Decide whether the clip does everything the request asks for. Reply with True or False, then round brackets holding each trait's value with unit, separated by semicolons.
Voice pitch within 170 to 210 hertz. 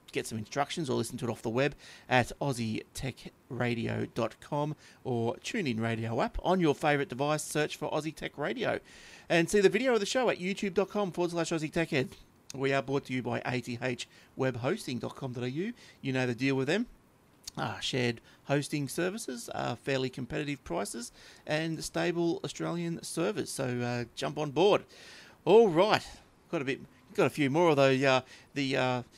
False (135 Hz)